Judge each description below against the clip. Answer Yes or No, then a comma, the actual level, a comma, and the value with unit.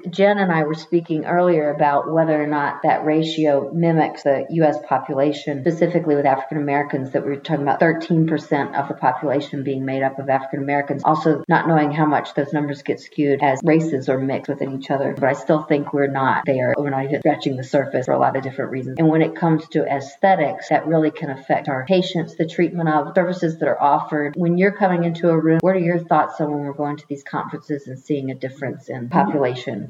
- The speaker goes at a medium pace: No, fast, 225 wpm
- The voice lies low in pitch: No, medium, 150 Hz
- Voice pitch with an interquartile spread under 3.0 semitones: Yes, narrow, 2.5 semitones